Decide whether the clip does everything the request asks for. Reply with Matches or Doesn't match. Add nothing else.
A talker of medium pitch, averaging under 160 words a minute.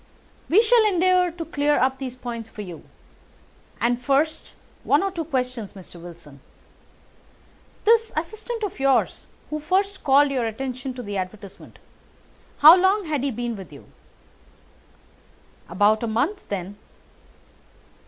Doesn't match